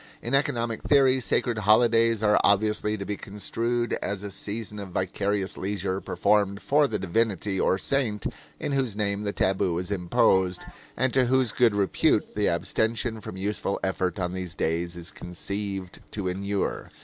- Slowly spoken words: No, average, 160 wpm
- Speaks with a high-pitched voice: No, low, 105 Hz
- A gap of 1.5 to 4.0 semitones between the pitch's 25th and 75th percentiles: Yes, average, 3.2 semitones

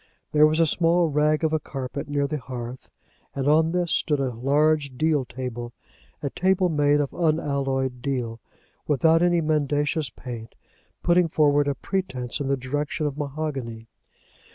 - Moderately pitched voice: Yes, medium, 145 Hz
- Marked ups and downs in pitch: No, average, 3.0 semitones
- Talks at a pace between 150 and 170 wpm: Yes, average, 155 wpm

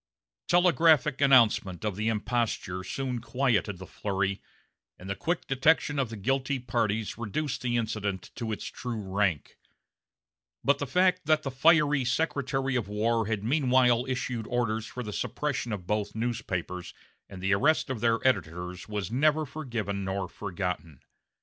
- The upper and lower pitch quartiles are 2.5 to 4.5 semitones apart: No, average, 4.9 semitones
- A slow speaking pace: No, average, 150 wpm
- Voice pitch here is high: No, low, 115 Hz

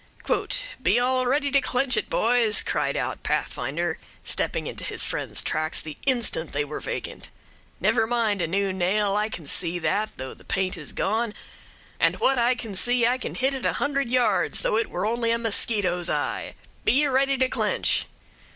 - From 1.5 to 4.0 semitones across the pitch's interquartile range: No, average, 4.9 semitones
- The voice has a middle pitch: No, high, 225 Hz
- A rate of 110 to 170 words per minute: No, average, 185 wpm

